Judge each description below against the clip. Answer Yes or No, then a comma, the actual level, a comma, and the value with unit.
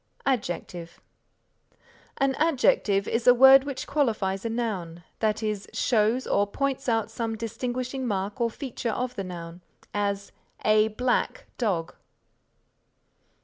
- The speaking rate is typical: No, slow, 125 wpm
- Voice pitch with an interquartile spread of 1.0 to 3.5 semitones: No, average, 4.1 semitones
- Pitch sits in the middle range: No, high, 225 Hz